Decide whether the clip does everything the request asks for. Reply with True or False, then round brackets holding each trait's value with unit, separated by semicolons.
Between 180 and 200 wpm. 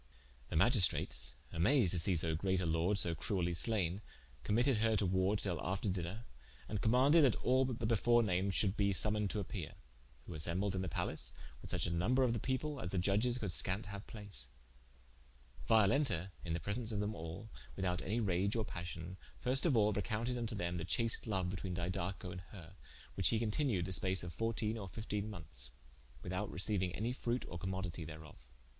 True (190 wpm)